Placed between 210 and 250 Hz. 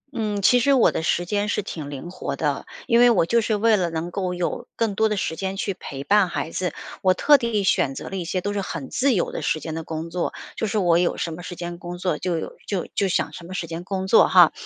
No: medium, 185 Hz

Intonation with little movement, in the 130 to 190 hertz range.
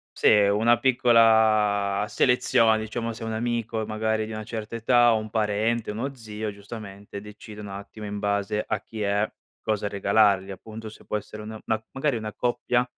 No: narrow, 1.7 semitones; low, 110 Hz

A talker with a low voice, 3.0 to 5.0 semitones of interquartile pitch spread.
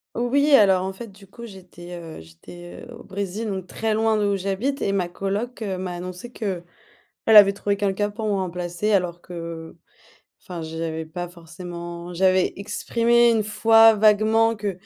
No: high, 195 Hz; average, 3.6 semitones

